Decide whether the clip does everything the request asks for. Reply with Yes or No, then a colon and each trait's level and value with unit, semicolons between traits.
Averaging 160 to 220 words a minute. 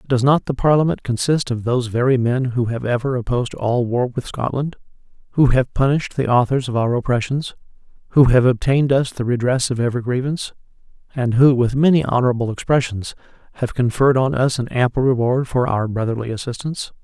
Yes: average, 180 wpm